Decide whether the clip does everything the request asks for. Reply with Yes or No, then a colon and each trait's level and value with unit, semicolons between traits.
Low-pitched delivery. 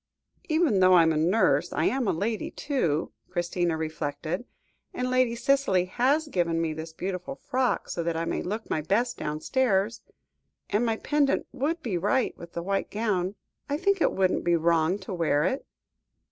No: high, 190 Hz